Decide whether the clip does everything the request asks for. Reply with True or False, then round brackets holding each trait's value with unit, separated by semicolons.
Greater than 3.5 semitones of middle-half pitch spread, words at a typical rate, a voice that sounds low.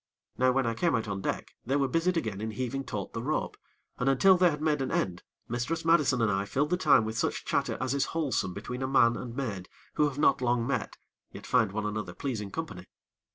False (4.8 semitones; 235 wpm; 125 Hz)